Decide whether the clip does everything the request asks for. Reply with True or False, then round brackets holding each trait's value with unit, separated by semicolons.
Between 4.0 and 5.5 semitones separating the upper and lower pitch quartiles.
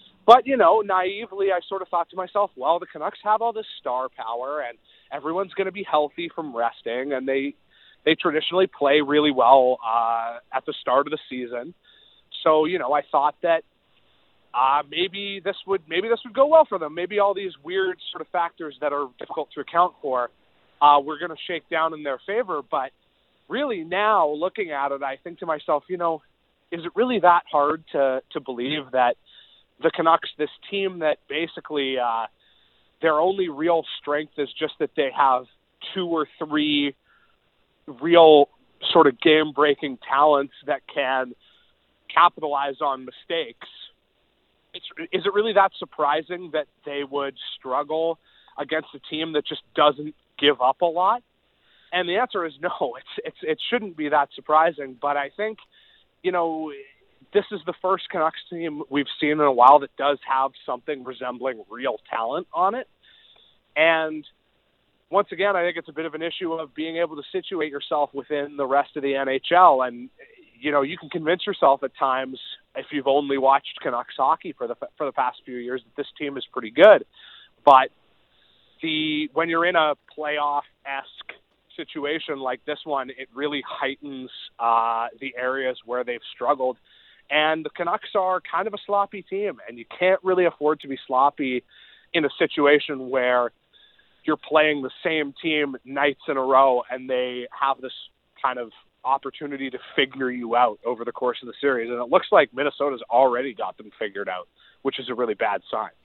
True (4.4 semitones)